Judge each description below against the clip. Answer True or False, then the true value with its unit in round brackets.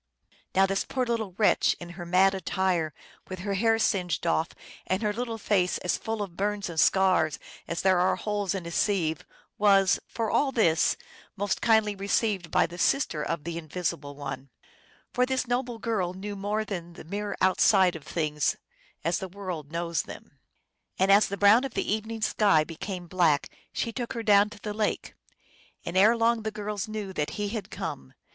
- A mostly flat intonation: False (3.7 semitones)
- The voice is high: True (195 Hz)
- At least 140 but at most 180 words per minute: False (190 wpm)